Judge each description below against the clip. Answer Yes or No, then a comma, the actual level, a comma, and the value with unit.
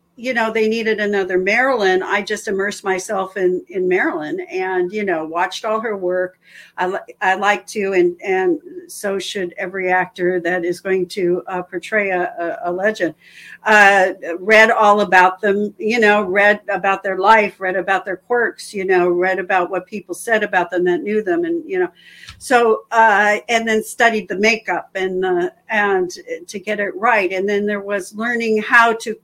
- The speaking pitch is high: Yes, high, 205 Hz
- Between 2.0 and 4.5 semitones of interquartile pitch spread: Yes, average, 3.1 semitones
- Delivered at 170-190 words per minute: Yes, average, 185 wpm